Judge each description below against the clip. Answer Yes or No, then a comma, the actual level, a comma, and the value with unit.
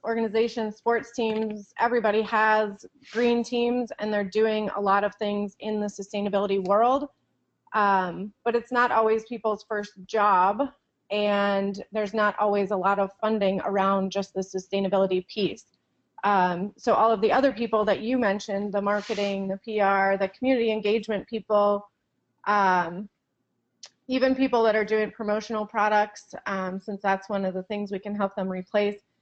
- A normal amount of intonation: No, narrow, 2.0 semitones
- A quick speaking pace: No, average, 160 wpm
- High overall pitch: Yes, high, 210 Hz